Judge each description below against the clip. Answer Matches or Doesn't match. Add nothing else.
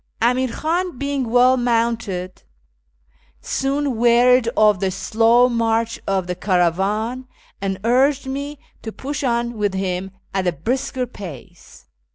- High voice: Matches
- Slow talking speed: Matches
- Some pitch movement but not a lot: Matches